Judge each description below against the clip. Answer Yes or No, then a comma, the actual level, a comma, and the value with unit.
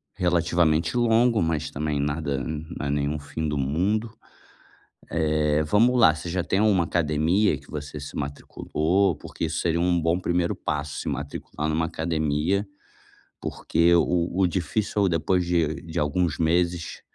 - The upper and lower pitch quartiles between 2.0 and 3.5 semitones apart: Yes, average, 2.8 semitones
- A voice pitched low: Yes, very low, 80 Hz